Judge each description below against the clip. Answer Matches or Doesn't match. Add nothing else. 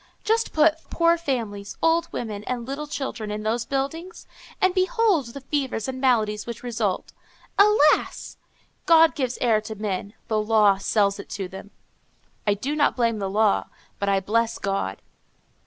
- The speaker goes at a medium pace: Matches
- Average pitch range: Doesn't match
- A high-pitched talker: Matches